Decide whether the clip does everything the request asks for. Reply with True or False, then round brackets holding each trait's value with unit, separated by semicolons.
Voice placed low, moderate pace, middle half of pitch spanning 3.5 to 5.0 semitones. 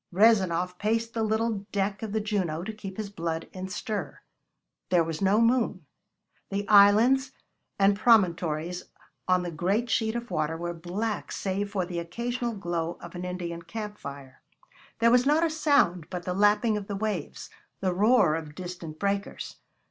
False (195 Hz; 170 wpm; 4.0 semitones)